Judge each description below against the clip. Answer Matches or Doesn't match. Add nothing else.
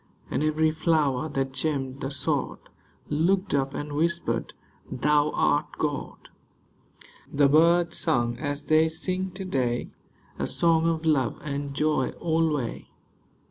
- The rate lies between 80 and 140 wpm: Matches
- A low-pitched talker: Doesn't match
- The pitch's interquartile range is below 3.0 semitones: Matches